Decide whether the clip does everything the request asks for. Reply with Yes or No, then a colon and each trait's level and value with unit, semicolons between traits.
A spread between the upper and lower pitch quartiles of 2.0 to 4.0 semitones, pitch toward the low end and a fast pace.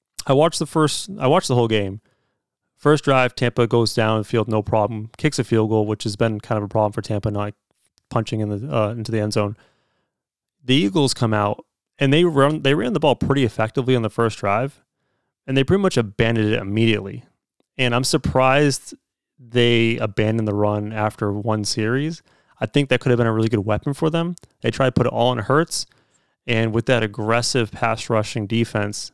Yes: average, 3.5 semitones; low, 115 Hz; fast, 210 wpm